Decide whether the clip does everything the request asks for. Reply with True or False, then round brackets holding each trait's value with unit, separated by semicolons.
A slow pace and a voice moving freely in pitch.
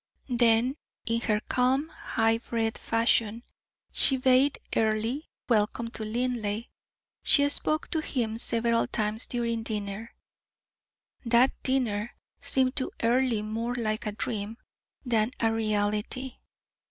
False (115 wpm; 2.7 semitones)